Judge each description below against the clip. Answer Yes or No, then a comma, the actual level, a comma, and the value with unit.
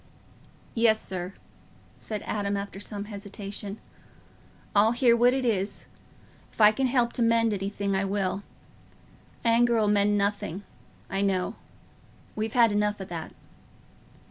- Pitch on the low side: No, high, 205 Hz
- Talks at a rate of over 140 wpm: No, slow, 135 wpm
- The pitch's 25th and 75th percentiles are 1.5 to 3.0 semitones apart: Yes, narrow, 2.4 semitones